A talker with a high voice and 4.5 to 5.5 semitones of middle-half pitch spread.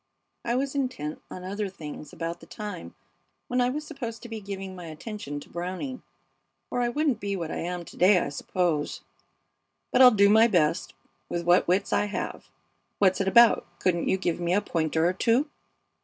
Yes: high, 195 Hz; average, 5.1 semitones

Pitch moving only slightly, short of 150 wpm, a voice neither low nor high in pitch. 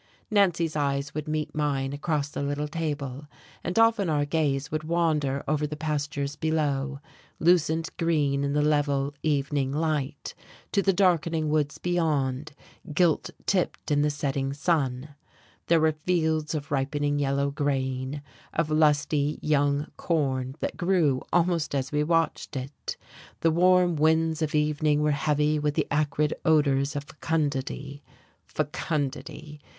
Yes: narrow, 2.0 semitones; average, 140 wpm; medium, 150 Hz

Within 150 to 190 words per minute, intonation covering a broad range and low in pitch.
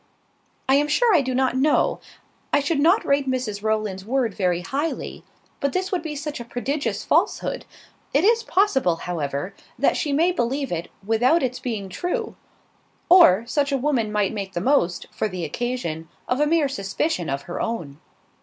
No: average, 180 wpm; wide, 7.0 semitones; very high, 255 Hz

